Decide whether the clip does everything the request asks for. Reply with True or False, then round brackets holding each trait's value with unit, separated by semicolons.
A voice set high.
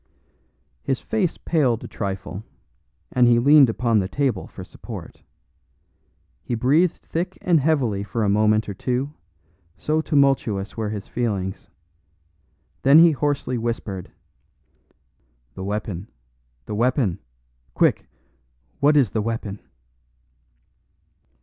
False (120 Hz)